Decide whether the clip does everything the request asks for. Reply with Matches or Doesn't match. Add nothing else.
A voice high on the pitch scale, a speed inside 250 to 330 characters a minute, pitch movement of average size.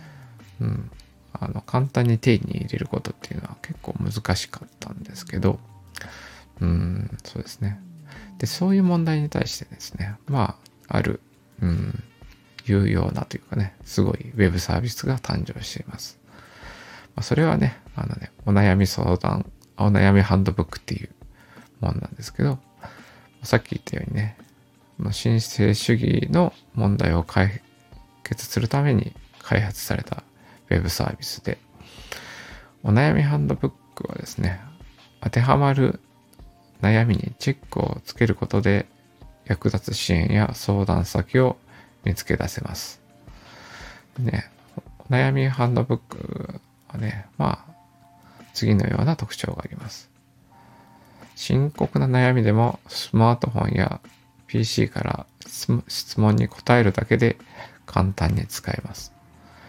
Doesn't match